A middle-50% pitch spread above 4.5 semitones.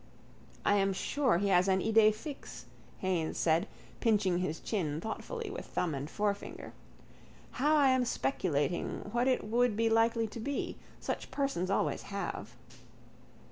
Yes: average, 5.1 semitones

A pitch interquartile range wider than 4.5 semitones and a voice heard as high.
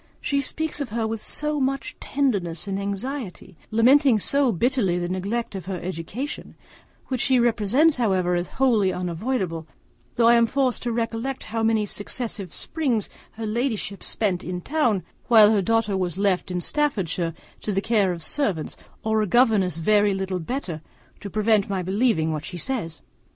Yes: average, 4.9 semitones; high, 215 Hz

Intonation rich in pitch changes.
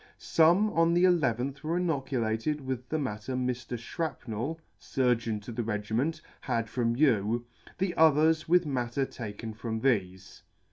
Yes: wide, 5.7 semitones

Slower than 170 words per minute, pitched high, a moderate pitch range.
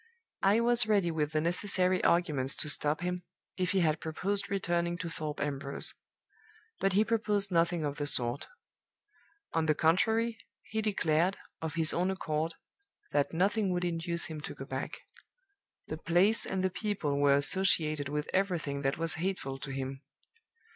No: average, 160 wpm; medium, 170 Hz; average, 4.2 semitones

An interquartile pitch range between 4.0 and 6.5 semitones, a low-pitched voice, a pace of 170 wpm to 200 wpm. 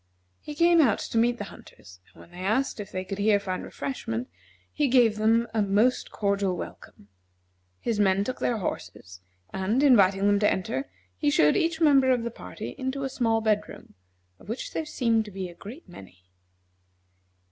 No: average, 4.9 semitones; high, 210 Hz; average, 185 wpm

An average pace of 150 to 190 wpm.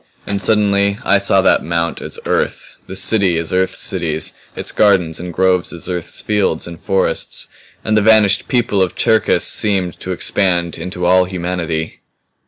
Yes: average, 165 wpm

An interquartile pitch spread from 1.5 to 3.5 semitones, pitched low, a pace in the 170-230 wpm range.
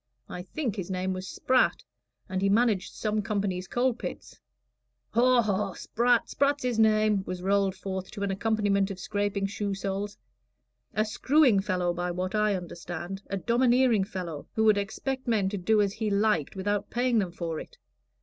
No: average, 2.7 semitones; high, 205 Hz; average, 175 wpm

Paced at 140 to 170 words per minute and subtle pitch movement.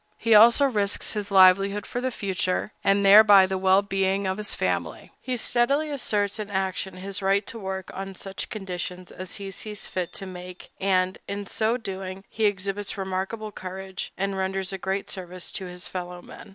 No: average, 185 wpm; narrow, 1.7 semitones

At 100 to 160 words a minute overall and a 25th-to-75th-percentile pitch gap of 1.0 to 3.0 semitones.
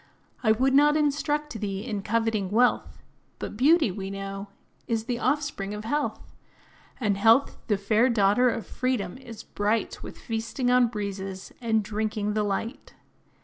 No: average, 150 wpm; average, 3.7 semitones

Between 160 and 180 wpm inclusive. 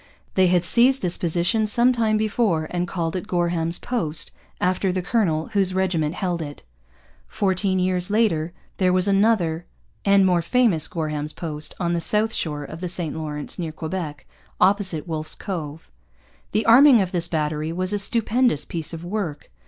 Yes: average, 170 wpm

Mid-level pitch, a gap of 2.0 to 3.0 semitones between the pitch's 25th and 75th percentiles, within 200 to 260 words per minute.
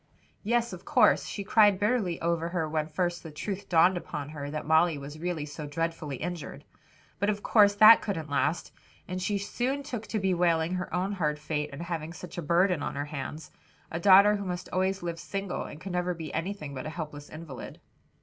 No: medium, 175 Hz; average, 3.9 semitones; fast, 205 wpm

